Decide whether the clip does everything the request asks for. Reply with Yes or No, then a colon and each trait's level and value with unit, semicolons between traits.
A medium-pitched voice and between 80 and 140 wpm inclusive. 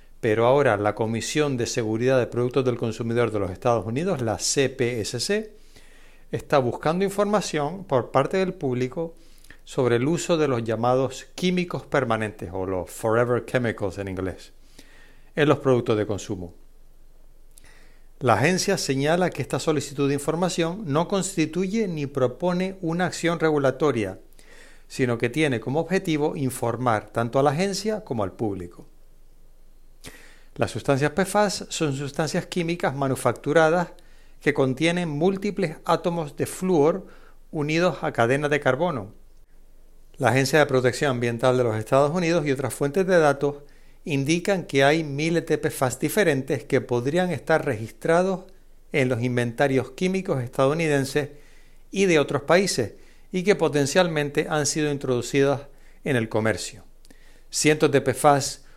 Yes: medium, 145 Hz; average, 135 wpm